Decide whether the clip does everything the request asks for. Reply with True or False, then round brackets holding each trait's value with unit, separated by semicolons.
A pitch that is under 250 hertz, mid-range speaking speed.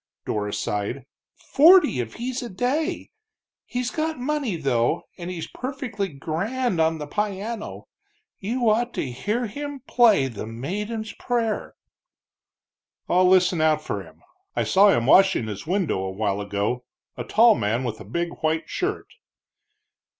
True (190 Hz; 145 wpm)